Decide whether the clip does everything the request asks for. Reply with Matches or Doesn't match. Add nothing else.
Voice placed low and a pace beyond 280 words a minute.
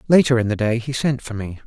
Matches